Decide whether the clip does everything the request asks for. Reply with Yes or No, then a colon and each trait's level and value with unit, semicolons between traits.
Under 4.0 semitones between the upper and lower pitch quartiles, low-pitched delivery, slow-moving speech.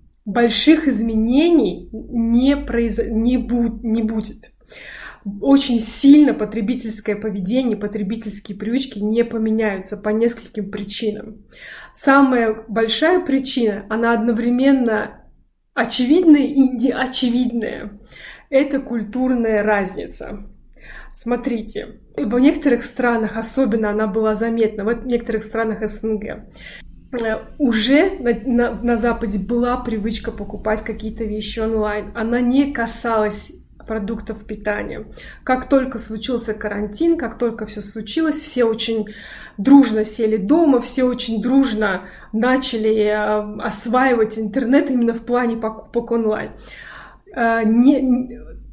No: narrow, 2.5 semitones; high, 230 Hz; slow, 105 wpm